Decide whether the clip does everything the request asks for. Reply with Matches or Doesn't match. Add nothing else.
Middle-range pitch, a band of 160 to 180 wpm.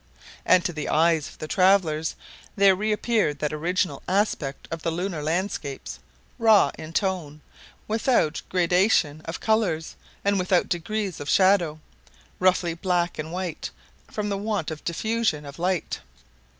Doesn't match